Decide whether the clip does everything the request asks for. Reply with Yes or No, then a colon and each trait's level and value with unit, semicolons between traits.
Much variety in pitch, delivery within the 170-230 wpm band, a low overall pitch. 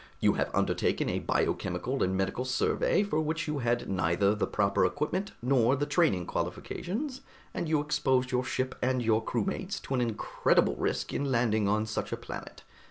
Yes: wide, 5.7 semitones; average, 175 wpm; low, 130 Hz